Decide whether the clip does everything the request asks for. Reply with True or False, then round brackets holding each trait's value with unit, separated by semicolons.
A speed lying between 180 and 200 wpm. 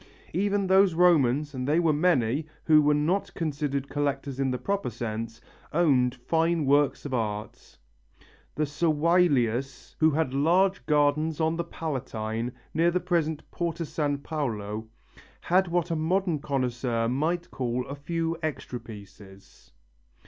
False (140 wpm)